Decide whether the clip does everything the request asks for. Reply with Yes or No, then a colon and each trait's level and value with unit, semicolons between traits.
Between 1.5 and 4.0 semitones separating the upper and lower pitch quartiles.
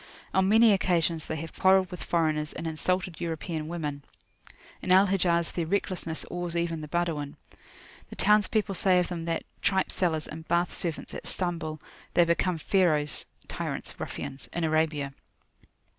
Yes: narrow, 2.5 semitones